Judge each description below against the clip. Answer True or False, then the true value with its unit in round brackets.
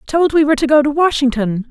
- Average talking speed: False (245 wpm)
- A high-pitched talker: True (280 Hz)